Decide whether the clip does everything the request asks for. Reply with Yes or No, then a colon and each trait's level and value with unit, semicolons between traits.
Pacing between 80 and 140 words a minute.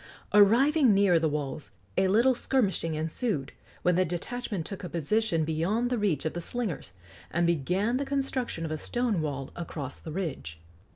No: average, 170 wpm